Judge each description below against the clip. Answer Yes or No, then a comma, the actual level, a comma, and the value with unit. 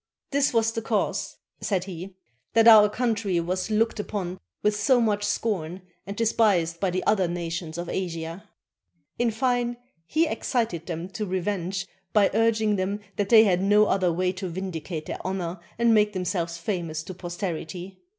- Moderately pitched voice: No, high, 195 Hz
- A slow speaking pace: No, average, 160 wpm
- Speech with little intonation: No, average, 3.6 semitones